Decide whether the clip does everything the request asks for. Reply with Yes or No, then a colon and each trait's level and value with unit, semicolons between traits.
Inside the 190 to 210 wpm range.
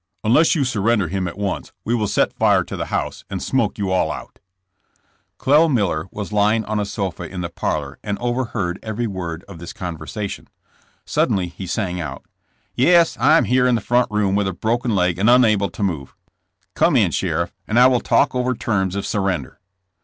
Yes: average, 200 wpm